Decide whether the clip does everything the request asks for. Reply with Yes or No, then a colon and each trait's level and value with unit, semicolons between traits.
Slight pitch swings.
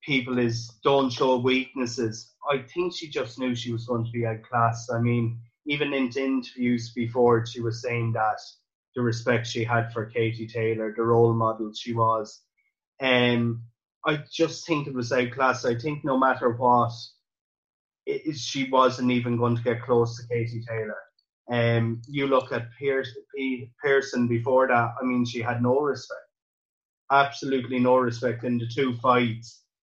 Yes: narrow, 2.1 semitones